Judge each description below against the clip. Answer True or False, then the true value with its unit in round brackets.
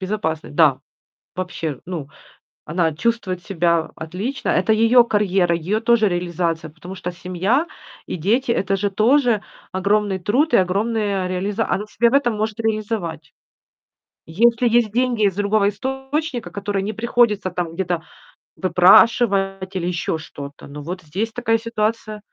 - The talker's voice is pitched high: True (200 Hz)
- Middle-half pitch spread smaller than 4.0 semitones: False (4.3 semitones)